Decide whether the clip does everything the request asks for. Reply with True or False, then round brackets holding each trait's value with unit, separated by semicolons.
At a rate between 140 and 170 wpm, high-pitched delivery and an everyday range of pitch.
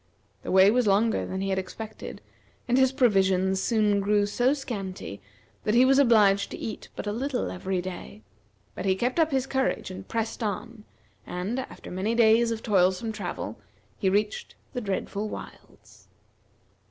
True (165 wpm; 210 Hz; 3.9 semitones)